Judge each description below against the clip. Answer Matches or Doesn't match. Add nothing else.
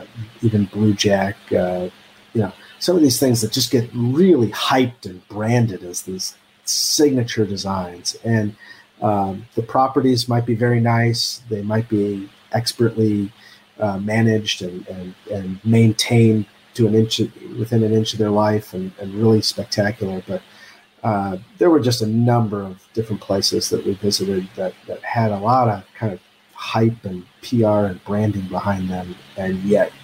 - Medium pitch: Doesn't match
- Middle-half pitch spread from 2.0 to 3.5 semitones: Matches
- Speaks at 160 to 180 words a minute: Matches